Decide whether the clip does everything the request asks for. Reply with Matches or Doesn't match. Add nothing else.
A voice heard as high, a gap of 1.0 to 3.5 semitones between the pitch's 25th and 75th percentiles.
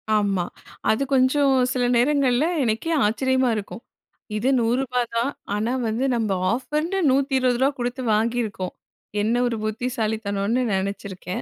Matches